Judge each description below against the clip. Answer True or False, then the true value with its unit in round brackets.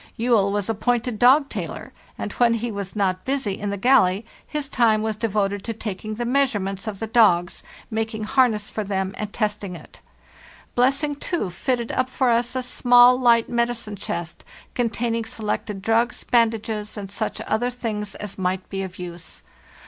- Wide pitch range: False (3.2 semitones)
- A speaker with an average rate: True (170 wpm)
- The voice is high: True (220 Hz)